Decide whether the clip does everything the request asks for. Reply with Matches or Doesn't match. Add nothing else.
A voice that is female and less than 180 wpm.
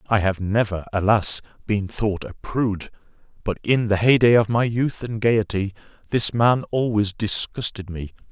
Doesn't match